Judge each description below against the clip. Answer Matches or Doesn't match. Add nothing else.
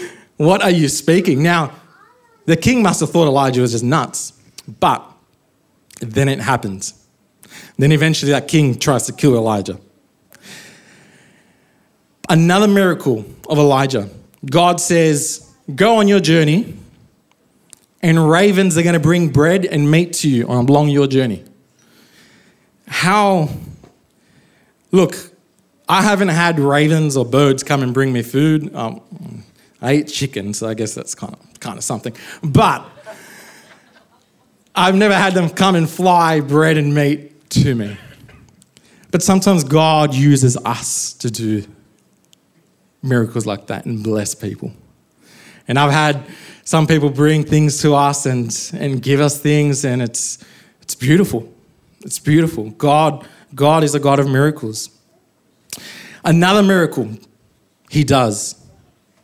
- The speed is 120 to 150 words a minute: Matches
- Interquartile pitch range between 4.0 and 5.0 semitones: Matches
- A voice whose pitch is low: Doesn't match